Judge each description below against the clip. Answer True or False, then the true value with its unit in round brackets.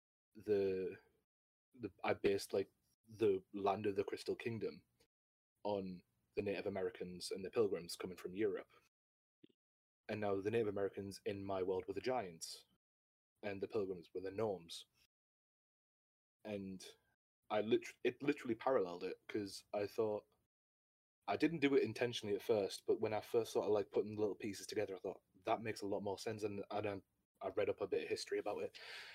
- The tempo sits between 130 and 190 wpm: True (175 wpm)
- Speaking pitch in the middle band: False (110 Hz)